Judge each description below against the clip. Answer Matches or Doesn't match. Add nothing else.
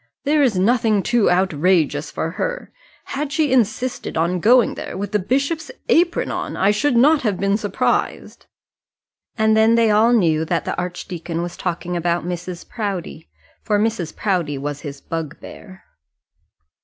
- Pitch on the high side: Matches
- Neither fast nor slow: Matches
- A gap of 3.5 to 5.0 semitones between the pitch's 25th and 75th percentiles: Doesn't match